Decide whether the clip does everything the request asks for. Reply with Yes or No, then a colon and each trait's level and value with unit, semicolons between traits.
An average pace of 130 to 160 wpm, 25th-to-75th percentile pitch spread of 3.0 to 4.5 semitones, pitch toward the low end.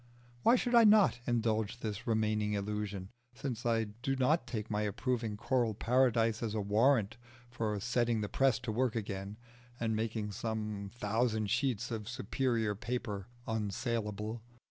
No: average, 145 wpm; narrow, 2.5 semitones; low, 110 Hz